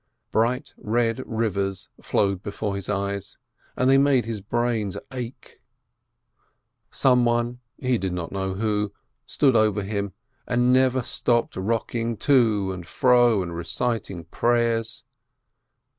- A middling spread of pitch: Yes, average, 3.5 semitones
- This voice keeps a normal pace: No, slow, 130 wpm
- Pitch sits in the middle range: No, low, 115 Hz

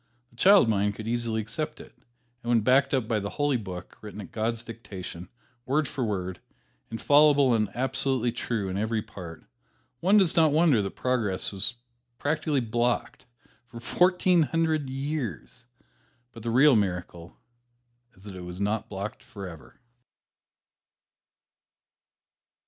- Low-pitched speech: Yes, low, 115 Hz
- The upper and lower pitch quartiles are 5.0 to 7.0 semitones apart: Yes, wide, 5.5 semitones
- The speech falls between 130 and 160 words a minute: Yes, average, 140 wpm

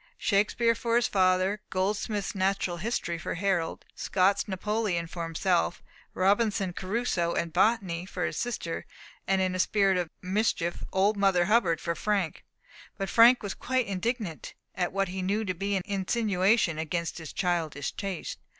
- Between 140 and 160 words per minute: Yes, average, 155 wpm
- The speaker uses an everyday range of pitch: Yes, average, 3.1 semitones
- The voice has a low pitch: No, high, 190 Hz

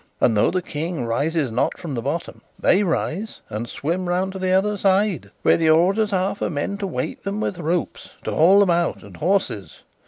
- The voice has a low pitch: No, medium, 175 Hz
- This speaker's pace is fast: Yes, fast, 210 wpm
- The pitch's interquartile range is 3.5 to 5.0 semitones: Yes, average, 3.9 semitones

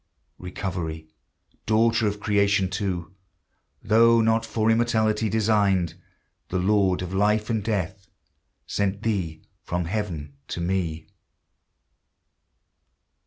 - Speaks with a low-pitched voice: Yes, low, 100 Hz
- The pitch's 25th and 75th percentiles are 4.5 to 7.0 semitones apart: No, average, 3.2 semitones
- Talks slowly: Yes, slow, 100 wpm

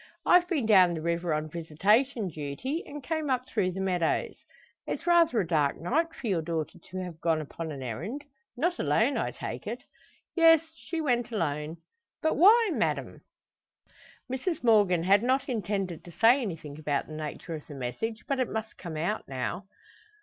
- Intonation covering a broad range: Yes, wide, 8.4 semitones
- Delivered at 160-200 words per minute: Yes, average, 180 wpm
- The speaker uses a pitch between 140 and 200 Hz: Yes, high, 190 Hz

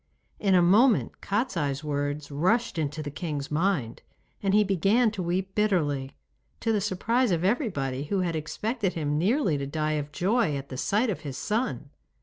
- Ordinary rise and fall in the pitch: No, wide, 6.2 semitones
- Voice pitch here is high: No, medium, 175 Hz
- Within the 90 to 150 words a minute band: No, average, 175 wpm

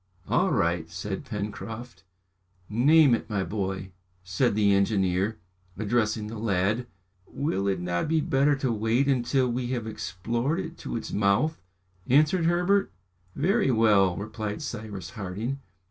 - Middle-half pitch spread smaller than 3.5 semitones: No, average, 5.1 semitones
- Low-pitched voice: Yes, low, 110 Hz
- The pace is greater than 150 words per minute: No, slow, 135 wpm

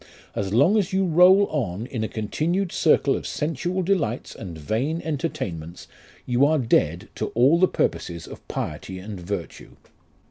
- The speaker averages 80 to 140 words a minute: No, average, 155 wpm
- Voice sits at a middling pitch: No, low, 130 Hz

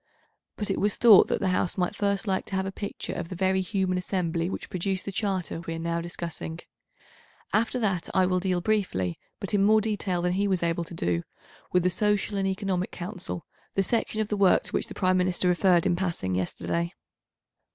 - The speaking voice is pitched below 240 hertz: Yes, medium, 185 Hz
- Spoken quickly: Yes, fast, 215 wpm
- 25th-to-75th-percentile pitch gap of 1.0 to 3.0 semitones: Yes, narrow, 2.5 semitones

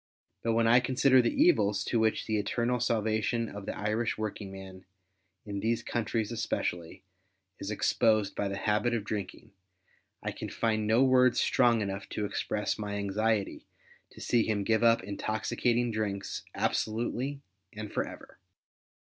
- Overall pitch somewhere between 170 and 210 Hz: No, low, 110 Hz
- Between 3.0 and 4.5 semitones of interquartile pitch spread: No, narrow, 2.4 semitones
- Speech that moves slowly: No, average, 155 wpm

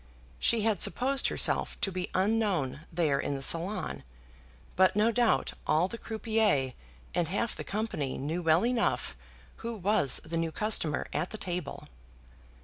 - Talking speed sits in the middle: Yes, average, 150 wpm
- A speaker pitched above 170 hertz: Yes, medium, 185 Hz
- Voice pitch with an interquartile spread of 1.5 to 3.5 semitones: No, average, 5.3 semitones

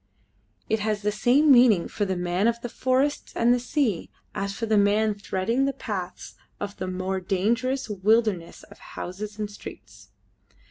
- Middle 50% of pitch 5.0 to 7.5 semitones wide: No, average, 3.9 semitones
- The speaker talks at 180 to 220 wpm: No, average, 170 wpm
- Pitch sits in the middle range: No, high, 210 Hz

